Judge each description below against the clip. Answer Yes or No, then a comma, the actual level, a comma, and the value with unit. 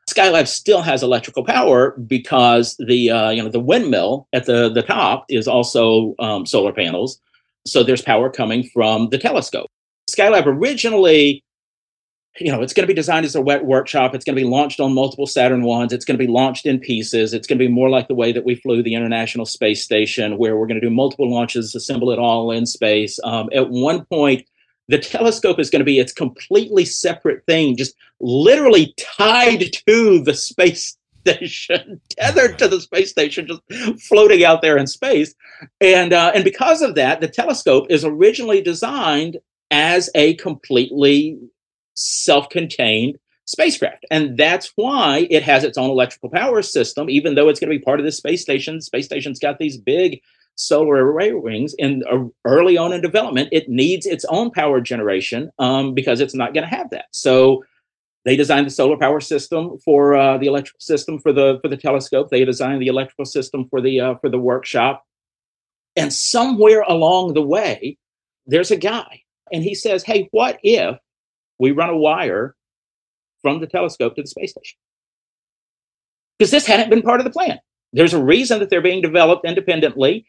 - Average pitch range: No, wide, 6.3 semitones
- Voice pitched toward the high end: No, medium, 145 Hz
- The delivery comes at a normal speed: Yes, average, 190 wpm